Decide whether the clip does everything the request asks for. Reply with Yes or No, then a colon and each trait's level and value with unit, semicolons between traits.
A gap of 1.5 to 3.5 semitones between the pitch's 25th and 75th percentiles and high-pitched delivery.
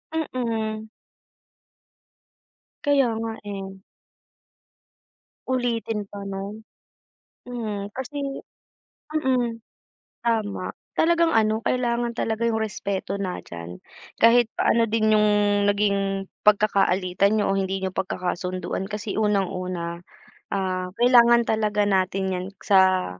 Yes: average, 3.2 semitones; high, 210 Hz